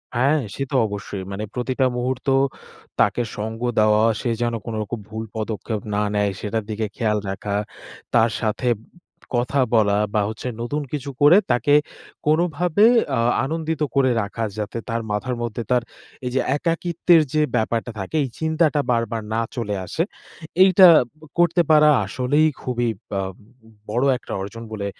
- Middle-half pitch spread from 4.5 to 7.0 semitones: Yes, average, 5.3 semitones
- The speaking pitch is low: Yes, low, 120 Hz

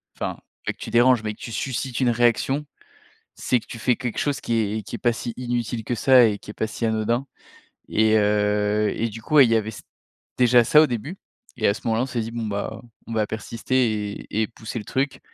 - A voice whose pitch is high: No, low, 115 Hz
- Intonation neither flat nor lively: No, narrow, 2.3 semitones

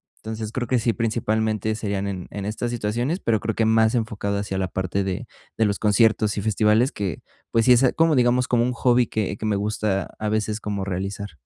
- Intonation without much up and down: Yes, narrow, 2.3 semitones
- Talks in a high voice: No, low, 110 Hz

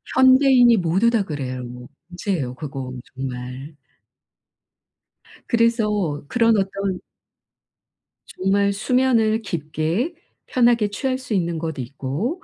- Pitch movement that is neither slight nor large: No, wide, 7.6 semitones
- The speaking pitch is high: Yes, high, 195 Hz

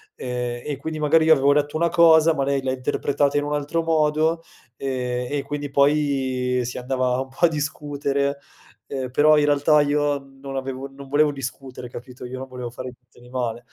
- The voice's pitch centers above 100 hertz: Yes, medium, 140 Hz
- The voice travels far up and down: No, narrow, 2.4 semitones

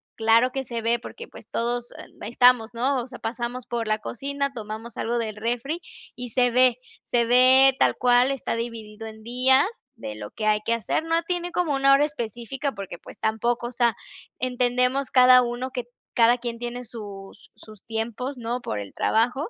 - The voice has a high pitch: Yes, high, 240 Hz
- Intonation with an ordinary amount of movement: No, narrow, 2.1 semitones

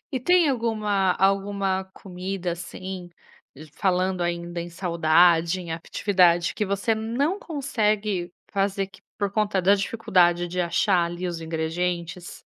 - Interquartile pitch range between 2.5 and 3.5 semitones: Yes, average, 2.9 semitones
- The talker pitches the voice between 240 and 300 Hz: No, medium, 185 Hz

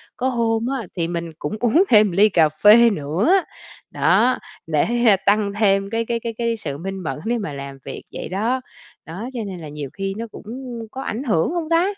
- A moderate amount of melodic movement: No, wide, 5.7 semitones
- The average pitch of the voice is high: Yes, high, 210 Hz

